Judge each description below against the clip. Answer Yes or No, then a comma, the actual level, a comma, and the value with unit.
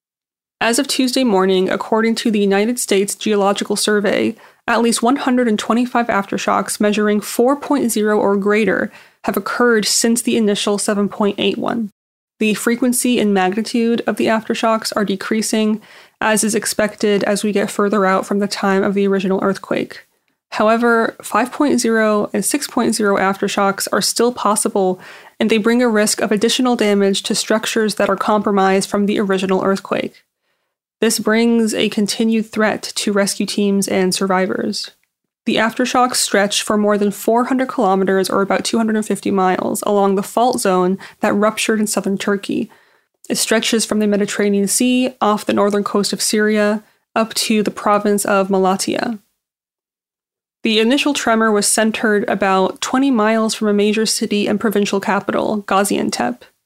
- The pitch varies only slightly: Yes, narrow, 2.3 semitones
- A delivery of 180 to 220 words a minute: No, average, 145 wpm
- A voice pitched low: No, high, 210 Hz